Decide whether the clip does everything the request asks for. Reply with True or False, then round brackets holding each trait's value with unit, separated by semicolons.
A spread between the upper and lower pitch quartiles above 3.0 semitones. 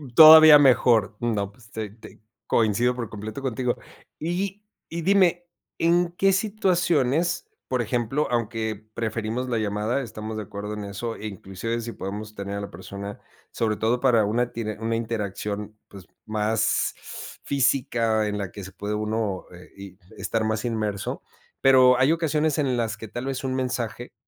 True (3.8 semitones)